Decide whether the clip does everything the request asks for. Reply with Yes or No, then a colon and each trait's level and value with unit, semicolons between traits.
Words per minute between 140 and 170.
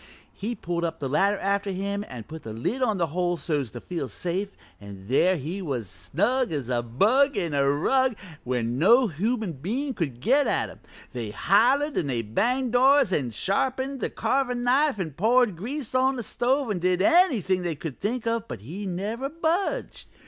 No: average, 190 wpm